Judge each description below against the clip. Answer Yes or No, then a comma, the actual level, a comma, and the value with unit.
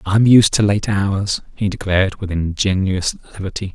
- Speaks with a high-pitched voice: No, low, 100 Hz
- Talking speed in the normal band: Yes, average, 175 wpm